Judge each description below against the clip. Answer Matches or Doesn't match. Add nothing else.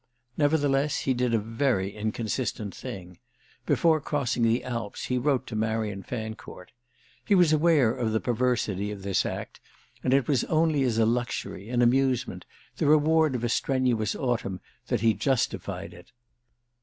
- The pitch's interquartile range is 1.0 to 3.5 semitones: Doesn't match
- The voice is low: Matches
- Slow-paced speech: Doesn't match